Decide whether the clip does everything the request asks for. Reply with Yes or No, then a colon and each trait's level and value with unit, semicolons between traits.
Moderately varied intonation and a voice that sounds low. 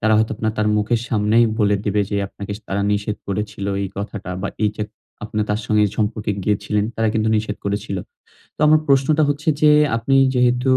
No: narrow, 2.1 semitones; low, 105 Hz